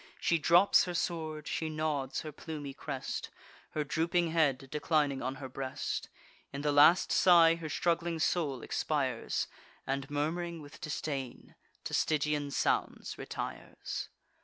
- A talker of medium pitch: Yes, medium, 150 Hz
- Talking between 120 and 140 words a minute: Yes, slow, 135 wpm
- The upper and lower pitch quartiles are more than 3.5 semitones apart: No, average, 2.9 semitones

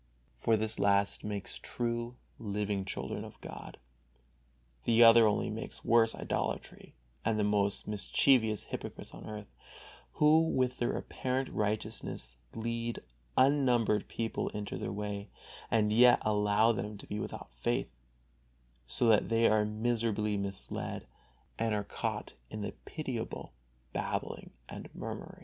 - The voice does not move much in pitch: Yes, narrow, 2.2 semitones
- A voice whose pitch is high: No, low, 110 Hz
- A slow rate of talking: Yes, slow, 130 wpm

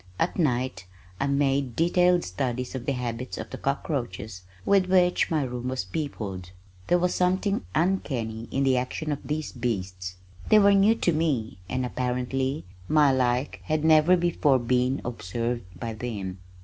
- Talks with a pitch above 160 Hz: No, low, 130 Hz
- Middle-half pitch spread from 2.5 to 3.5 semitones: No, average, 5.0 semitones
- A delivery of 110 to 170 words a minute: Yes, average, 160 wpm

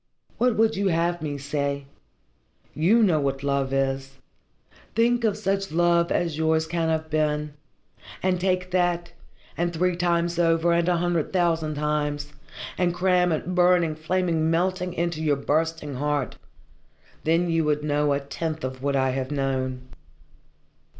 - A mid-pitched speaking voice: Yes, medium, 165 Hz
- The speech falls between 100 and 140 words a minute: No, average, 155 wpm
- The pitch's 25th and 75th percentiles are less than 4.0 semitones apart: Yes, average, 3.2 semitones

